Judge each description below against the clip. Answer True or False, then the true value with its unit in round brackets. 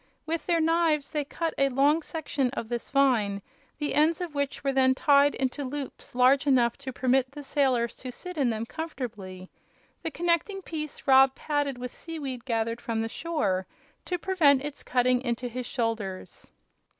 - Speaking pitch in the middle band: False (270 Hz)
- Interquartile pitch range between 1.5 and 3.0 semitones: False (3.7 semitones)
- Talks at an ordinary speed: True (175 wpm)